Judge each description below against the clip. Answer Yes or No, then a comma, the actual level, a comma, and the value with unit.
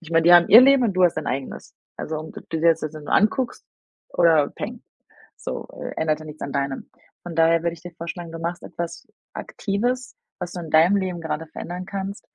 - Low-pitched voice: No, medium, 170 Hz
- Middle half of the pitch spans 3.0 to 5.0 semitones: No, narrow, 2.6 semitones